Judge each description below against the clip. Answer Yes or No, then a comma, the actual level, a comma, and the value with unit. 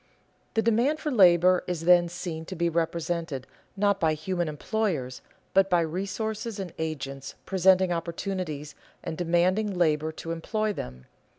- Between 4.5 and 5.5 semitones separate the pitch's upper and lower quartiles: No, average, 3.2 semitones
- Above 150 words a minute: No, average, 140 wpm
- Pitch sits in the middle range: Yes, medium, 175 Hz